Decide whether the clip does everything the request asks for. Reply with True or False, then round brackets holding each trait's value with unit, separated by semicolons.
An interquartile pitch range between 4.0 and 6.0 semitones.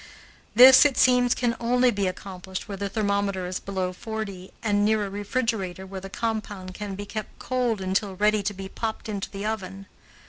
False (2.5 semitones)